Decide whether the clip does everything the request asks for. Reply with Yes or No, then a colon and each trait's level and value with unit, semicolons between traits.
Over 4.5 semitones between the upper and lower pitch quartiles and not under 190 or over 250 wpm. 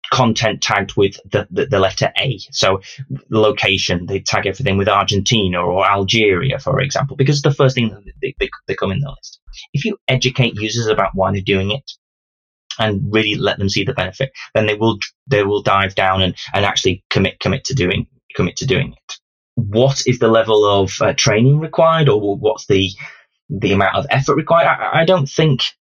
Yes: wide, 5.4 semitones; average, 195 wpm